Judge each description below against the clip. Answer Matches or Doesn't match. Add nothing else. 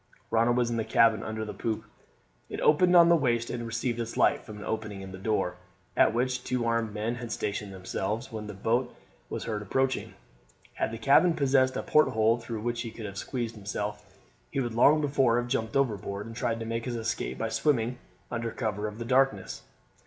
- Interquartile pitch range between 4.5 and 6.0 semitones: Doesn't match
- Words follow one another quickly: Matches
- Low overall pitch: Matches